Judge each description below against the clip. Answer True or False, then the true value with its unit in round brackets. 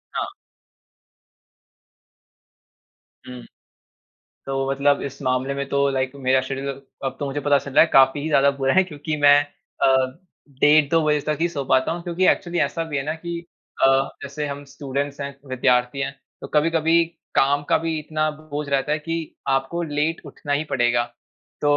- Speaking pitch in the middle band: True (145 Hz)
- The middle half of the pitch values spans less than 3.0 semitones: True (2.4 semitones)